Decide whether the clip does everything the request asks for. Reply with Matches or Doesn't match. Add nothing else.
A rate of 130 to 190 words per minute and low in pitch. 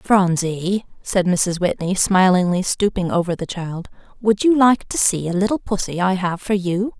Doesn't match